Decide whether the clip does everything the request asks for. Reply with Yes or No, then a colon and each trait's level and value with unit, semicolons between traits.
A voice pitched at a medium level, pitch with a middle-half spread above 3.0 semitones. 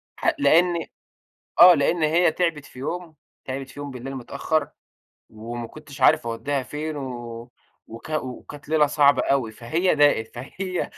Yes: medium, 145 Hz; average, 4.0 semitones